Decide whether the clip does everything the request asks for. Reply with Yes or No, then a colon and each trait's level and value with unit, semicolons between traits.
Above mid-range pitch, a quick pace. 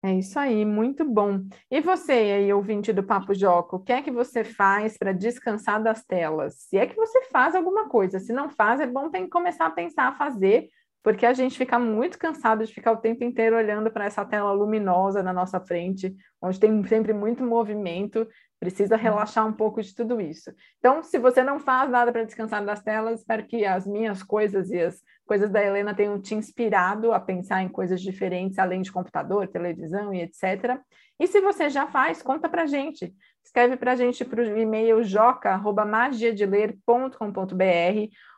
Yes: high, 220 Hz; fast, 190 wpm